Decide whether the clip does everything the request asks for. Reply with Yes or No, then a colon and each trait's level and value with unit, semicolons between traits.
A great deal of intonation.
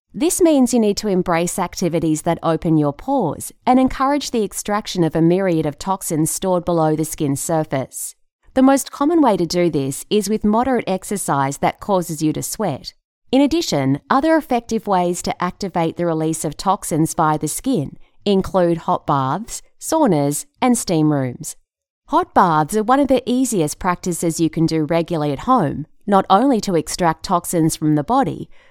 Yes: wide, 6.8 semitones